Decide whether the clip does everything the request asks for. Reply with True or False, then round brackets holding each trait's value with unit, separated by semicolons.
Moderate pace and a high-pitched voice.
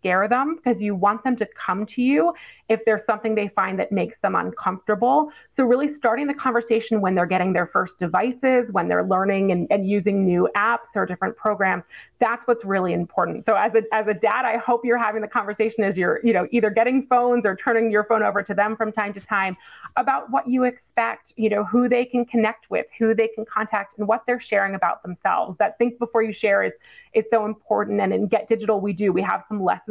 False (230 wpm; 220 Hz)